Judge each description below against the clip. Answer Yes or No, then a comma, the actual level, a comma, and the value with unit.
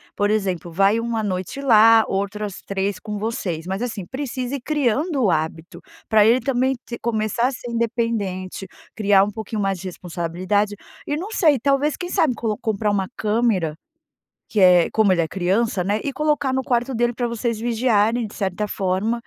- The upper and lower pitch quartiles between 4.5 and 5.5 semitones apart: No, average, 3.8 semitones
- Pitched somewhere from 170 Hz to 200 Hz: No, high, 215 Hz